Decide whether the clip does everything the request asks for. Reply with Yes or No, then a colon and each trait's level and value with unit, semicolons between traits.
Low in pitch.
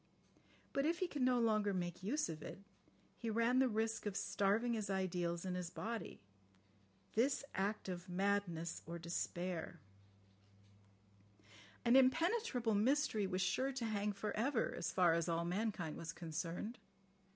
No: high, 205 Hz